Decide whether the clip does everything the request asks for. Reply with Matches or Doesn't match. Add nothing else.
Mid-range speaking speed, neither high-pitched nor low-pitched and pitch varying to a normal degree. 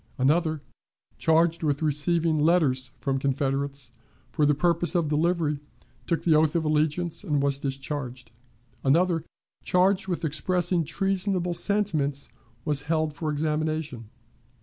Doesn't match